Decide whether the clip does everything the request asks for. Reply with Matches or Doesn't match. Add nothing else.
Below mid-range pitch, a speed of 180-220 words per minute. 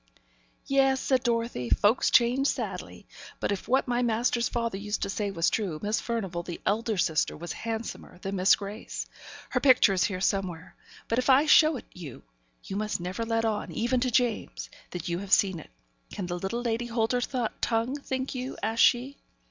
Doesn't match